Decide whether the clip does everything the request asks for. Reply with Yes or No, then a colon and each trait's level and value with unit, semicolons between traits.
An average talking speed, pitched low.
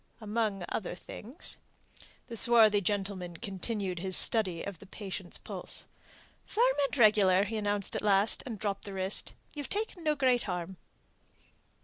No: average, 145 wpm; high, 205 Hz